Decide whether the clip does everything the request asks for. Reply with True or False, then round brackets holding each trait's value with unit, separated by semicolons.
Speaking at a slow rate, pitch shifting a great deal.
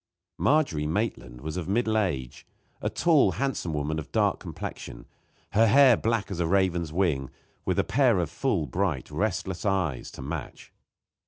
False (160 wpm; 6.3 semitones)